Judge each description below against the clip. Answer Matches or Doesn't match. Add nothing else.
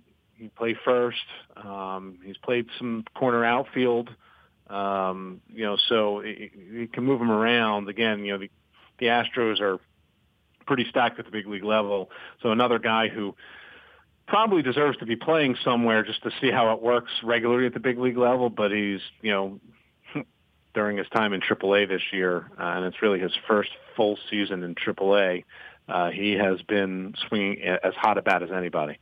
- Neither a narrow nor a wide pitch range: Matches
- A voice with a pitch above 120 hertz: Doesn't match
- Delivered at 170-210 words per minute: Matches